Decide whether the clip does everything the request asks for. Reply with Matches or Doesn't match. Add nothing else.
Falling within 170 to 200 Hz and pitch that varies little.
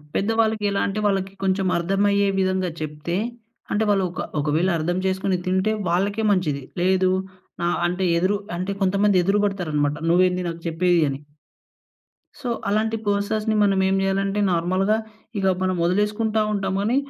Matches